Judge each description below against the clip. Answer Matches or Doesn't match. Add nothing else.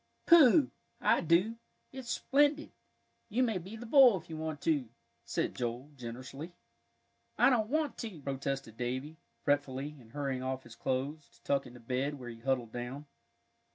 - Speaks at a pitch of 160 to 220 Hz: Doesn't match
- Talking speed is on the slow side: Doesn't match